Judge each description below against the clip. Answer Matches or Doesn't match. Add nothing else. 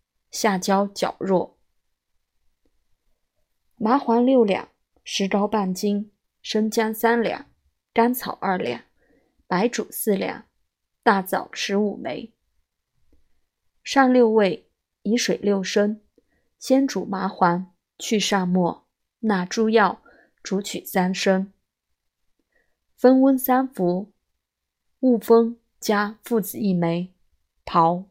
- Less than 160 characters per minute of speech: Matches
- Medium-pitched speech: Doesn't match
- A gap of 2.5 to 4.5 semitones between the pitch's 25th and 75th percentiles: Matches